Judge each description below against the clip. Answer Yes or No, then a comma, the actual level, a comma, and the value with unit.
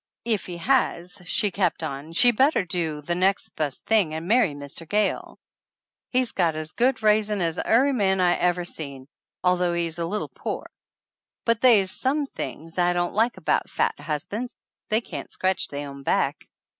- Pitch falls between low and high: Yes, medium, 180 Hz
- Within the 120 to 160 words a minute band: No, average, 175 wpm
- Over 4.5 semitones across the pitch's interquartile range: Yes, average, 5.0 semitones